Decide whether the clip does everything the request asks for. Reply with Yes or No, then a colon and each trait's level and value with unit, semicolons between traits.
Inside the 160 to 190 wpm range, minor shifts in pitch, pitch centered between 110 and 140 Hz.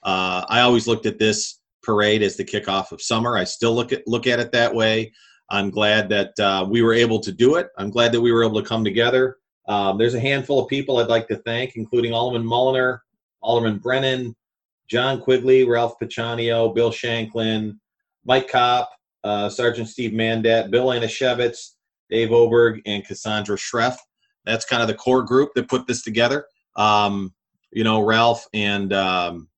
Yes: average, 185 wpm; narrow, 2.3 semitones; low, 115 Hz